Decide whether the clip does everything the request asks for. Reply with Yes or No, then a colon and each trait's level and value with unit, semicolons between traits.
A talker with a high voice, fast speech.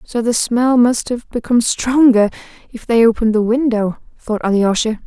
No: high, 230 Hz; average, 165 wpm